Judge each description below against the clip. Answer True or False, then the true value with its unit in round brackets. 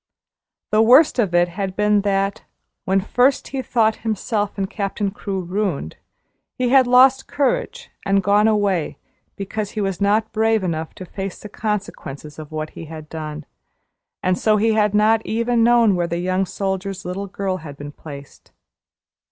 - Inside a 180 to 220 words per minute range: False (170 wpm)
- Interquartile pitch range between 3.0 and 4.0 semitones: True (3.4 semitones)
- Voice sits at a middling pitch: False (200 Hz)